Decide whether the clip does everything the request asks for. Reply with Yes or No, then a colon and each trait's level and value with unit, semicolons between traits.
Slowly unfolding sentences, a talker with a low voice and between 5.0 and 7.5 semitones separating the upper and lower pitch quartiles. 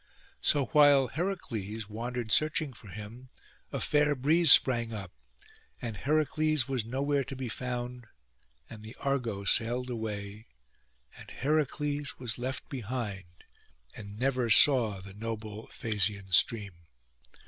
No: slow, 125 wpm; low, 120 Hz; average, 4.3 semitones